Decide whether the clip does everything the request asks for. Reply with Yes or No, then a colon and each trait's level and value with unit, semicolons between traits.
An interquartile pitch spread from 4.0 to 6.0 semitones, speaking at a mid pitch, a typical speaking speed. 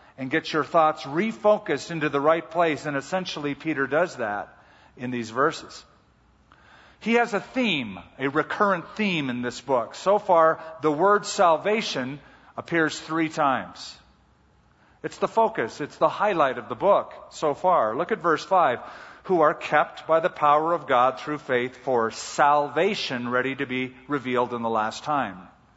Yes: average, 5.1 semitones; medium, 155 Hz; average, 165 wpm